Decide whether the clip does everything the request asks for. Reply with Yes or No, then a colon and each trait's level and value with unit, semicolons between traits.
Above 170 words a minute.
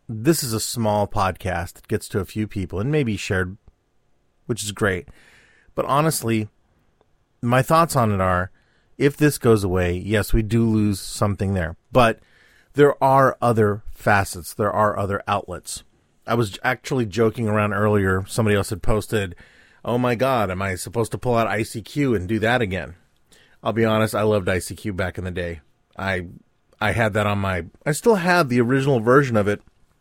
Yes: average, 180 wpm